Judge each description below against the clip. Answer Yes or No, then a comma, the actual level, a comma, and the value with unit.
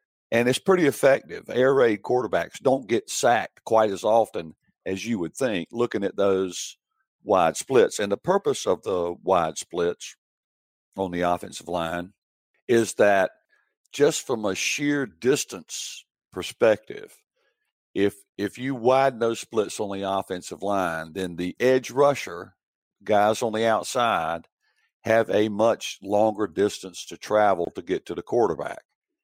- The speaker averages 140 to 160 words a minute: Yes, average, 145 wpm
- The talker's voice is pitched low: Yes, low, 105 Hz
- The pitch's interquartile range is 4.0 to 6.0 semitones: Yes, average, 4.8 semitones